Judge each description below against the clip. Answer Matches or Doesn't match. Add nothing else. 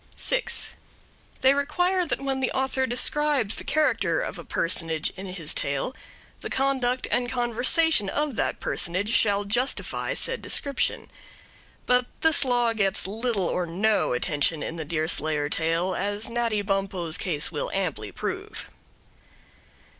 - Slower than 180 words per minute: Matches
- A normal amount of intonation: Doesn't match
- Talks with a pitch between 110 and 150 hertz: Doesn't match